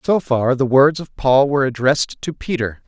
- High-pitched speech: No, low, 135 Hz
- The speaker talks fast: Yes, fast, 210 wpm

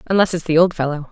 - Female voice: Yes, female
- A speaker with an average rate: No, fast, 270 wpm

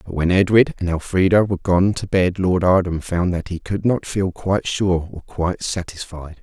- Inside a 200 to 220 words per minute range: Yes, fast, 205 wpm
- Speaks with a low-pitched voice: Yes, very low, 90 Hz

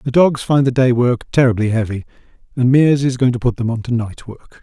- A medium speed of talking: No, fast, 245 wpm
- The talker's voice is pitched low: Yes, low, 125 Hz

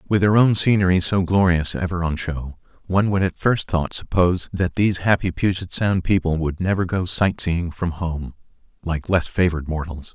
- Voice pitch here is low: Yes, very low, 90 Hz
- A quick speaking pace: No, average, 185 wpm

